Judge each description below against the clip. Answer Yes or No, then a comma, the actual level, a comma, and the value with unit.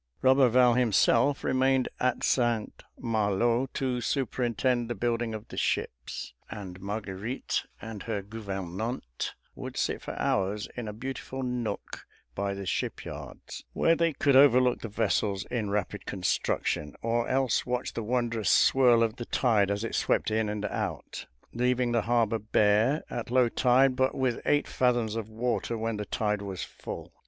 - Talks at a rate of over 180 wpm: No, average, 155 wpm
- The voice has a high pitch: No, low, 115 Hz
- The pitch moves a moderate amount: Yes, average, 3.2 semitones